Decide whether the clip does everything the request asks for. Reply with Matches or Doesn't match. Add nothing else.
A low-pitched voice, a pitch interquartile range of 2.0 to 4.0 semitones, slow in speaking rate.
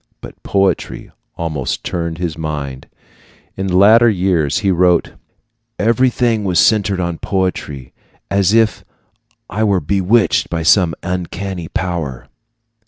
Matches